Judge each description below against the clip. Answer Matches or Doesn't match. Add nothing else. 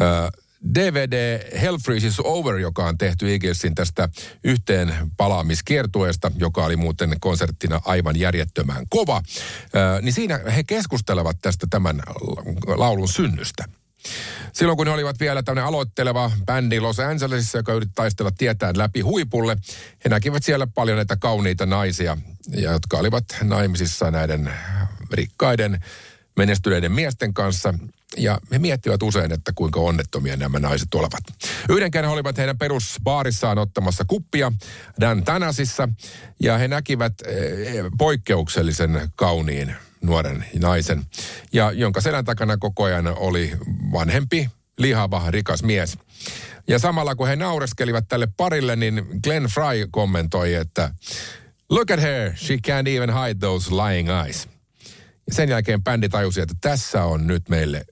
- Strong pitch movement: Matches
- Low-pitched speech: Matches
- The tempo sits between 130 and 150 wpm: Matches